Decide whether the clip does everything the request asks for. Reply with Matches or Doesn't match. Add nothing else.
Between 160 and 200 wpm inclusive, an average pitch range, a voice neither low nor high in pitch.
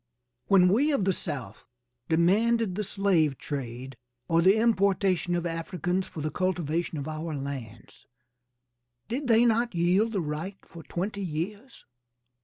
Doesn't match